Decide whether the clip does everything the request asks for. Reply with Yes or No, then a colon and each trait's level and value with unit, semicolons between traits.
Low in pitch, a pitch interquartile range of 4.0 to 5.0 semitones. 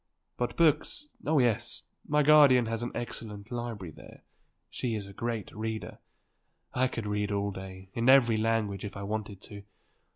No: low, 110 Hz; average, 3.2 semitones